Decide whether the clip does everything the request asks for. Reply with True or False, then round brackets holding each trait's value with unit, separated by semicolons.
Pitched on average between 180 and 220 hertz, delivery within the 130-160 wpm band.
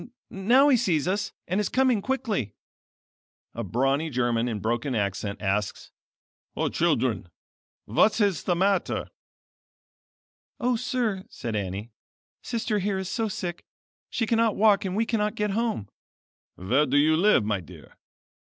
True (185 Hz; 145 wpm)